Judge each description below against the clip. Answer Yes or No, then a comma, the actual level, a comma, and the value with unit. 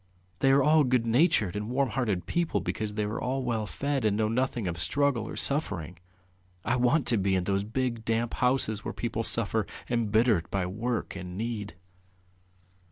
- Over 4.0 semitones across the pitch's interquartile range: No, average, 3.6 semitones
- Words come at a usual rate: Yes, average, 175 wpm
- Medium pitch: No, low, 115 Hz